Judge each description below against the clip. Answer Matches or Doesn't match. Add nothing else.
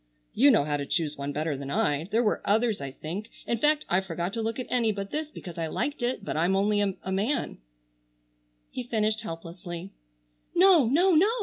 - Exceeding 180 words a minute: Matches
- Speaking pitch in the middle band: Doesn't match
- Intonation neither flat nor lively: Doesn't match